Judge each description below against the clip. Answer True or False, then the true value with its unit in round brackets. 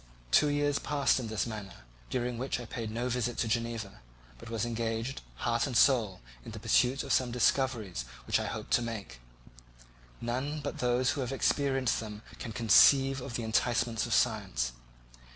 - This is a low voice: True (120 Hz)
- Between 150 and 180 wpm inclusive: True (175 wpm)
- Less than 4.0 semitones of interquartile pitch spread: True (2.8 semitones)